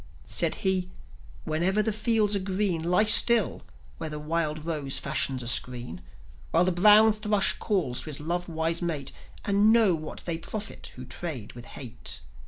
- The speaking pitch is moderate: Yes, medium, 170 Hz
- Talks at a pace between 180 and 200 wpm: No, average, 170 wpm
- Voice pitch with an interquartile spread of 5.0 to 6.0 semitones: Yes, wide, 5.4 semitones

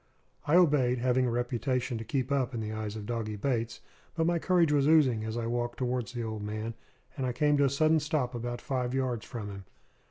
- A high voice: No, low, 125 Hz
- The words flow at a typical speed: No, fast, 225 wpm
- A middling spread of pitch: Yes, average, 3.4 semitones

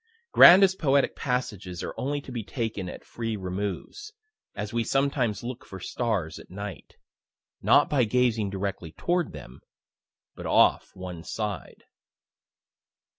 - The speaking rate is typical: No, slow, 130 wpm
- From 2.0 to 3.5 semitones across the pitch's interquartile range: No, average, 5.2 semitones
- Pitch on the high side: No, low, 110 Hz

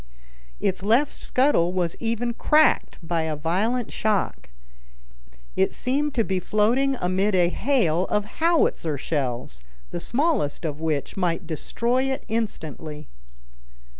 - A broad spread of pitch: Yes, wide, 7.1 semitones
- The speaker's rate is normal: No, slow, 125 wpm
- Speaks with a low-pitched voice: No, high, 195 Hz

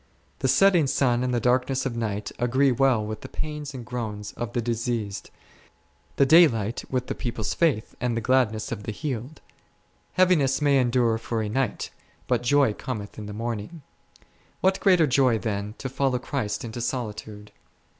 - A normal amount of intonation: Yes, average, 3.6 semitones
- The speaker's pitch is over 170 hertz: No, low, 120 Hz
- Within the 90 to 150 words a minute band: No, average, 170 wpm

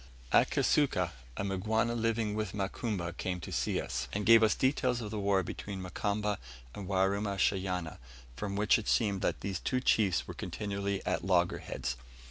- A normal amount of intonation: No, narrow, 2.3 semitones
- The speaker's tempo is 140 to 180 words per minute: Yes, average, 165 wpm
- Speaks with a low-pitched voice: Yes, low, 100 Hz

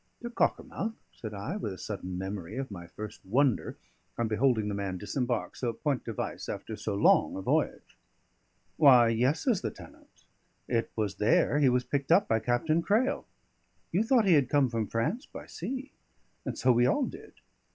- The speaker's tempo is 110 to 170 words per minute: No, average, 185 wpm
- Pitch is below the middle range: Yes, low, 125 Hz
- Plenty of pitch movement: Yes, wide, 6.6 semitones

